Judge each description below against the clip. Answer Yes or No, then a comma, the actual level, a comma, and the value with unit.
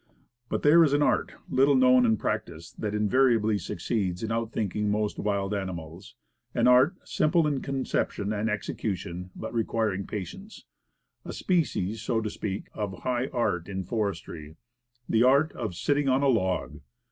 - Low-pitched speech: Yes, low, 110 Hz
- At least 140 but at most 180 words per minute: Yes, average, 160 wpm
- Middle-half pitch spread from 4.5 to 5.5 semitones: Yes, average, 4.8 semitones